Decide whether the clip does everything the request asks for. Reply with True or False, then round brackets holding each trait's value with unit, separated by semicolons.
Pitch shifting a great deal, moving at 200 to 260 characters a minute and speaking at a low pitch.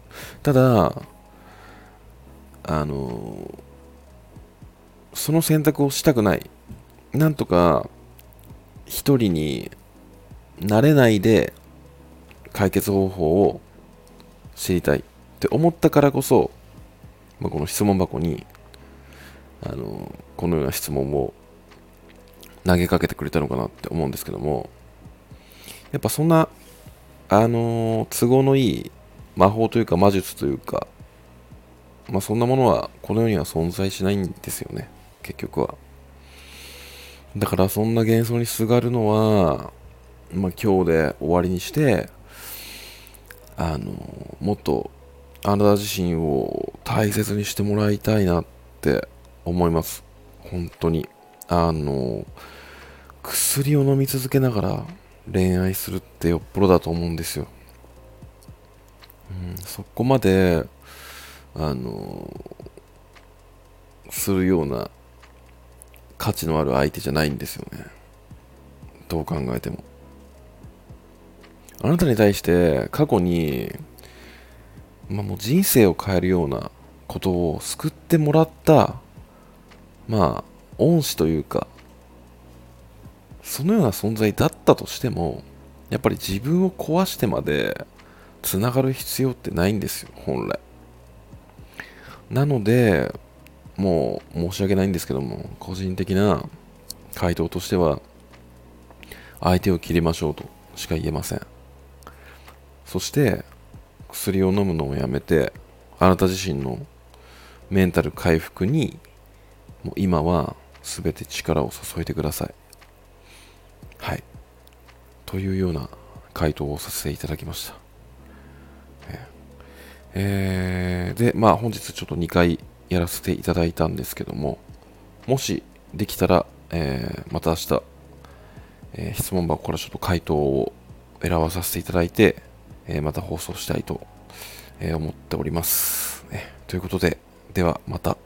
True (6.7 semitones; 230 characters per minute; 85 Hz)